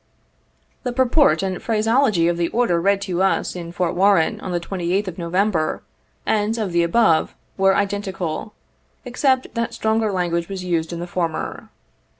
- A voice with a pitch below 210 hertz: Yes, high, 190 Hz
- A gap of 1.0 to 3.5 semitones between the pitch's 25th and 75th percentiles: No, average, 4.2 semitones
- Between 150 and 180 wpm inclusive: Yes, average, 160 wpm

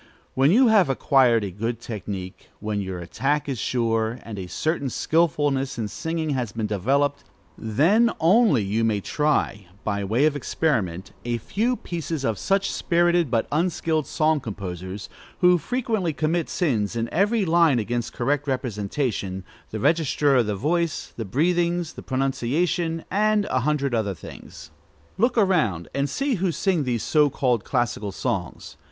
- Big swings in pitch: Yes, wide, 7.2 semitones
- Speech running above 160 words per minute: No, average, 155 wpm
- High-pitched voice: No, low, 135 Hz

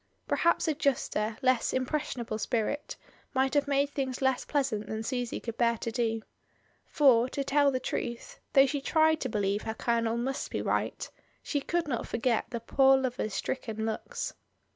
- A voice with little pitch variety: No, average, 3.4 semitones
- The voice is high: Yes, very high, 255 Hz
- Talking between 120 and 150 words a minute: No, average, 170 wpm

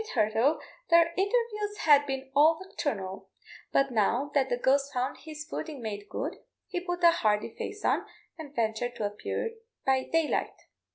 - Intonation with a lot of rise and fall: Yes, wide, 5.9 semitones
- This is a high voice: Yes, very high, 280 Hz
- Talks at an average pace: Yes, average, 160 wpm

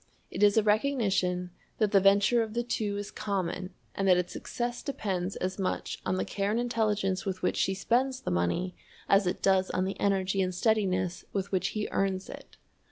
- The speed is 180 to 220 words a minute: Yes, average, 200 wpm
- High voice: Yes, high, 195 Hz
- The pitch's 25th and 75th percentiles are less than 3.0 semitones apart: Yes, narrow, 2.5 semitones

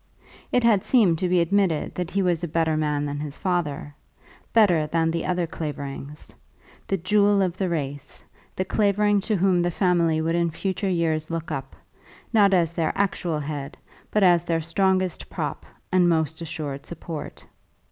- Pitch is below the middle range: No, medium, 170 Hz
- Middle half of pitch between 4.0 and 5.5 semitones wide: No, average, 3.2 semitones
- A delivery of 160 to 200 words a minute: Yes, average, 170 wpm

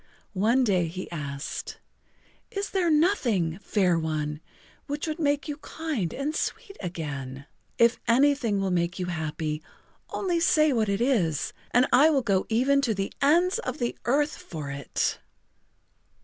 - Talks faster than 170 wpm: No, average, 150 wpm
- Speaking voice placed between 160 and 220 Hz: No, high, 230 Hz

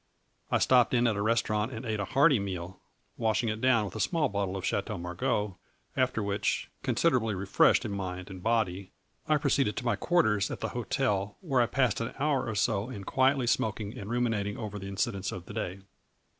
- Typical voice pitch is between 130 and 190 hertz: No, low, 110 Hz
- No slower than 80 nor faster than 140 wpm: No, average, 200 wpm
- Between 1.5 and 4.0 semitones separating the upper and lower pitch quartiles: Yes, average, 3.7 semitones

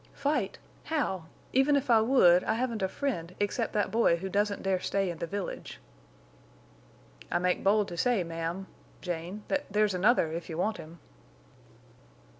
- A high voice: Yes, high, 195 Hz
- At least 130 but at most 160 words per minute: Yes, average, 155 wpm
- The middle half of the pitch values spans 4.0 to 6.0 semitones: Yes, average, 4.7 semitones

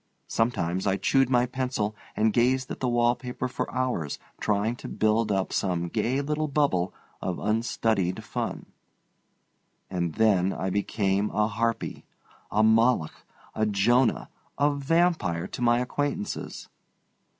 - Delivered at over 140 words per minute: No, slow, 135 wpm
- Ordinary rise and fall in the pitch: Yes, average, 4.4 semitones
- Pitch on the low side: Yes, low, 110 Hz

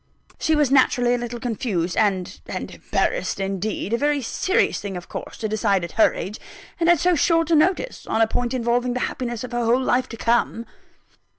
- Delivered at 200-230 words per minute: Yes, fast, 205 wpm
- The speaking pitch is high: Yes, high, 240 Hz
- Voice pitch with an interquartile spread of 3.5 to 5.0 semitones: Yes, average, 4.2 semitones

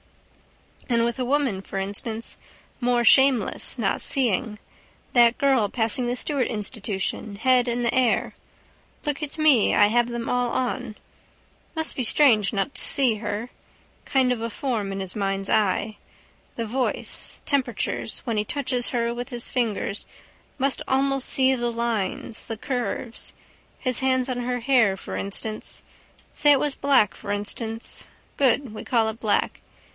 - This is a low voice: No, high, 240 Hz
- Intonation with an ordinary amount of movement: Yes, average, 3.1 semitones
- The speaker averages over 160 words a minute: No, average, 155 wpm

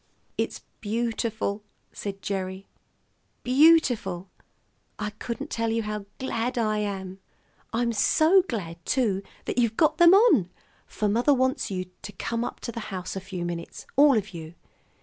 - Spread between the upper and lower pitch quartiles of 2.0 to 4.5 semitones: Yes, average, 4.1 semitones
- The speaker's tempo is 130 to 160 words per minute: Yes, average, 150 wpm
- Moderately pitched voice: No, high, 215 Hz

